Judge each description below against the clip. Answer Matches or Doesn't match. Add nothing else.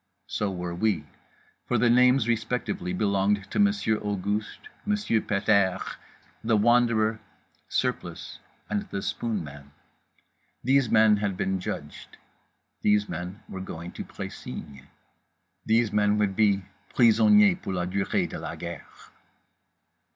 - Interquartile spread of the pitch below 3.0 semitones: Doesn't match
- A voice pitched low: Matches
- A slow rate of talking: Matches